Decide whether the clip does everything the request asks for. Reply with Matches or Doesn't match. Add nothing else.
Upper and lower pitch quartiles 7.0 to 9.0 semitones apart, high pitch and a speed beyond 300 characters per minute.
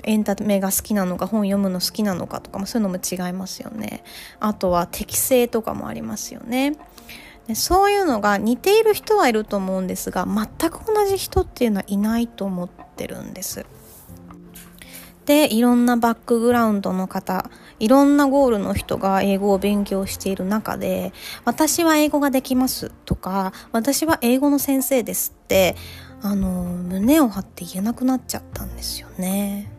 Doesn't match